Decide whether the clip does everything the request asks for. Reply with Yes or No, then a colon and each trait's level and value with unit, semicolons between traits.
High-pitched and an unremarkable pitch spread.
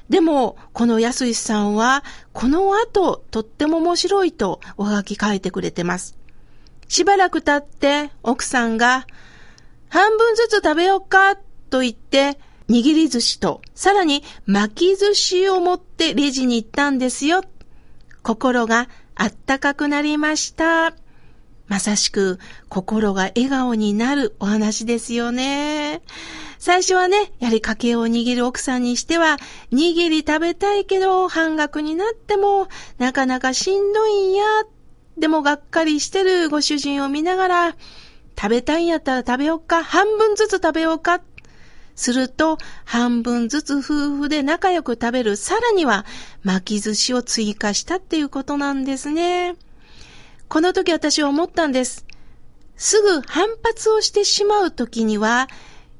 No: very high, 295 Hz; wide, 6.8 semitones